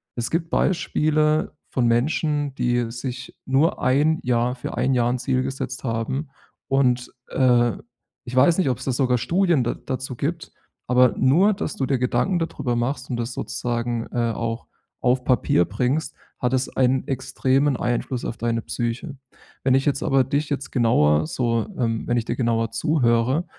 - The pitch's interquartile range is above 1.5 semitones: Yes, narrow, 2.6 semitones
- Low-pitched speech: Yes, low, 130 Hz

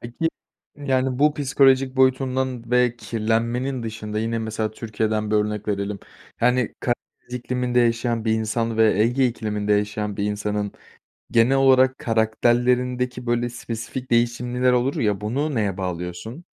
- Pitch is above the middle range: No, low, 120 Hz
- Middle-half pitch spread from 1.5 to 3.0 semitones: Yes, average, 2.7 semitones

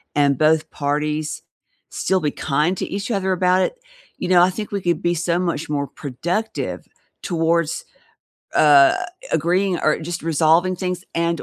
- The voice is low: No, medium, 170 Hz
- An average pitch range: Yes, average, 3.1 semitones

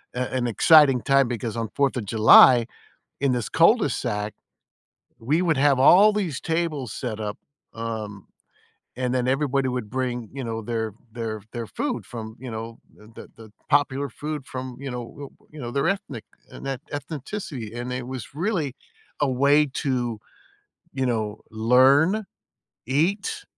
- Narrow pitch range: No, average, 3.9 semitones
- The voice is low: Yes, low, 130 Hz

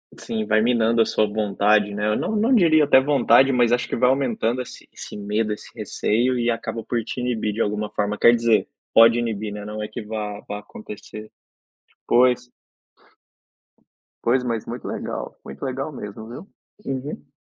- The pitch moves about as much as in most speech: Yes, average, 3.0 semitones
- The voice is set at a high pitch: No, low, 115 Hz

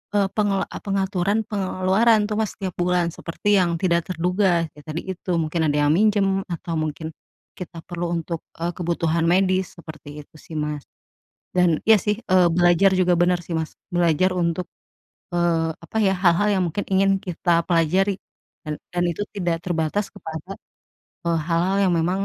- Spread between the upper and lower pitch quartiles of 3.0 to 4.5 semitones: No, narrow, 2.4 semitones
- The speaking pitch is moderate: Yes, medium, 175 Hz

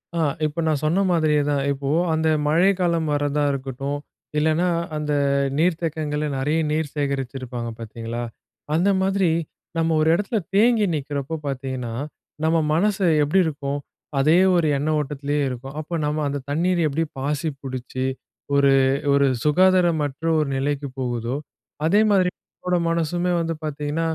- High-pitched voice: No, medium, 150 Hz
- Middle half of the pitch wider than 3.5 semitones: No, average, 3.2 semitones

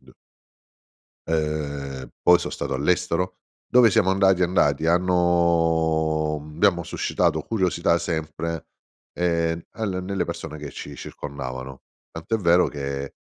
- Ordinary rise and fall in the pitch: Yes, average, 3.1 semitones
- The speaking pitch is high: No, very low, 80 Hz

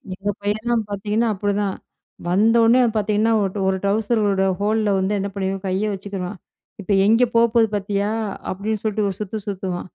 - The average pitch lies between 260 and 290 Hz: No, high, 205 Hz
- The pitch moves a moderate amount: No, narrow, 1.9 semitones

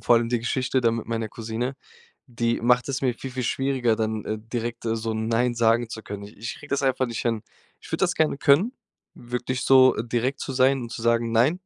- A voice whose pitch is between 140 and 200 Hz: No, low, 120 Hz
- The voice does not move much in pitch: Yes, narrow, 2.2 semitones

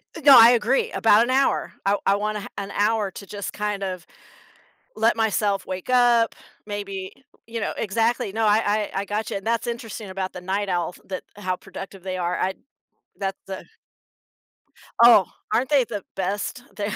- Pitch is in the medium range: No, high, 205 Hz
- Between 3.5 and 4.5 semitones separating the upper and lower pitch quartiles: No, average, 2.9 semitones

